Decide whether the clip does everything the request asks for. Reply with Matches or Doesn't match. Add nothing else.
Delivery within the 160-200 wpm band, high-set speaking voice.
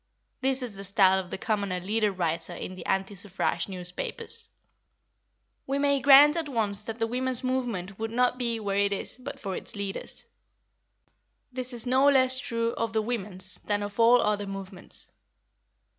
Matches